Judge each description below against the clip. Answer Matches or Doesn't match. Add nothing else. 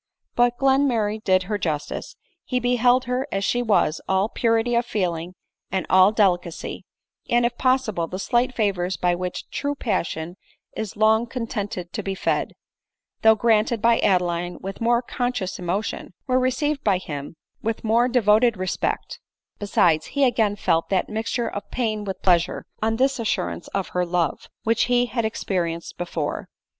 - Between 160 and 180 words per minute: Matches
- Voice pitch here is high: Matches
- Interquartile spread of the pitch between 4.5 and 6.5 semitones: Matches